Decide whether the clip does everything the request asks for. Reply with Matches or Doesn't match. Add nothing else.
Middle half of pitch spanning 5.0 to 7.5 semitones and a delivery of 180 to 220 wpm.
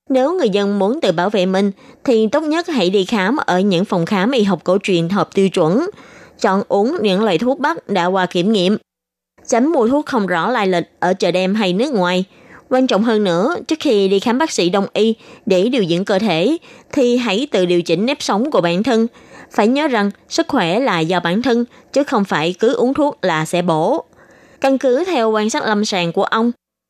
Doesn't match